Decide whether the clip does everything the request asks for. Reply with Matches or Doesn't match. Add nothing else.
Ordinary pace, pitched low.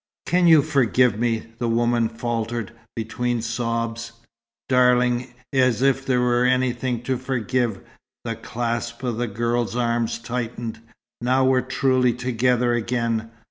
Doesn't match